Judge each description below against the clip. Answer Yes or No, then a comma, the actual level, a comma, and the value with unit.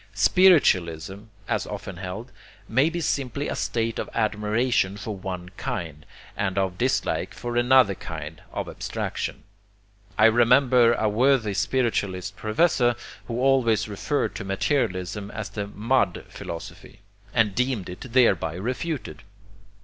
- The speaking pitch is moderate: No, low, 110 Hz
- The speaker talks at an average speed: No, slow, 125 wpm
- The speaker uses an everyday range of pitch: Yes, average, 4.9 semitones